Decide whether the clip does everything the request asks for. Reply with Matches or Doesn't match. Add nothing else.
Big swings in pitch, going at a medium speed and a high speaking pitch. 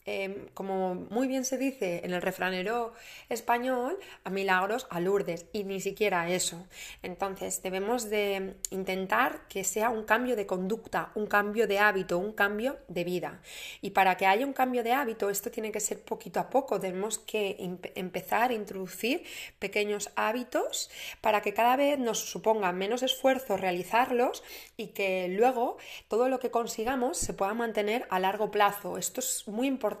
Doesn't match